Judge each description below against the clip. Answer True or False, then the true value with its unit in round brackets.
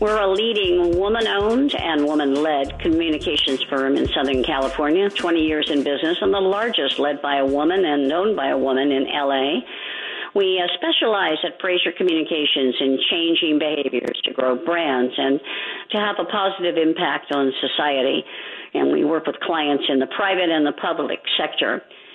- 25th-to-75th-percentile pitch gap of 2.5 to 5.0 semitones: False (5.6 semitones)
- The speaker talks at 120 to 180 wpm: True (165 wpm)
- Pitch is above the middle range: False (155 Hz)